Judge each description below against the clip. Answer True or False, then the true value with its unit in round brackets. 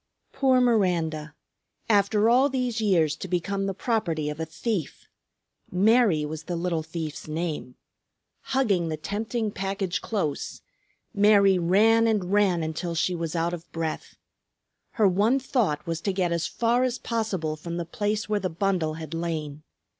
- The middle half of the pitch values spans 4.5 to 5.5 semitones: True (4.8 semitones)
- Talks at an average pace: True (155 wpm)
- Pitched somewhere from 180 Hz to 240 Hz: True (185 Hz)